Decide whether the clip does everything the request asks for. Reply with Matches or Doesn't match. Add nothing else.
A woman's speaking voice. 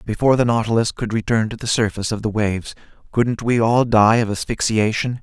Doesn't match